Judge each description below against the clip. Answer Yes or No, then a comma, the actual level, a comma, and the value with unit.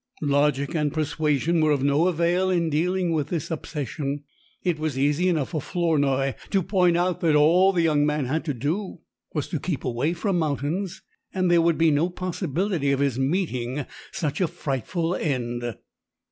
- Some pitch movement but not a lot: Yes, average, 3.6 semitones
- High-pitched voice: No, medium, 155 Hz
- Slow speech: No, average, 175 wpm